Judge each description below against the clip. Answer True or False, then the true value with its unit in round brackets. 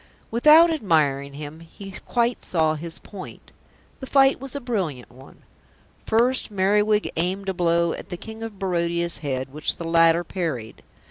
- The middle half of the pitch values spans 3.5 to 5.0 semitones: False (5.6 semitones)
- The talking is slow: False (155 wpm)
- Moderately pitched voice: True (175 Hz)